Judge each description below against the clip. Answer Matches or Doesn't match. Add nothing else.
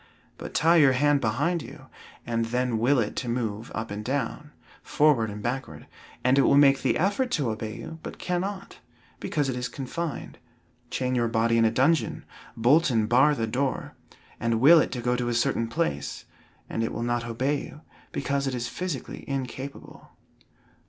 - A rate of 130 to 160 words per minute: Doesn't match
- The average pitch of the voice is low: Matches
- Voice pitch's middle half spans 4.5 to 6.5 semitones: Doesn't match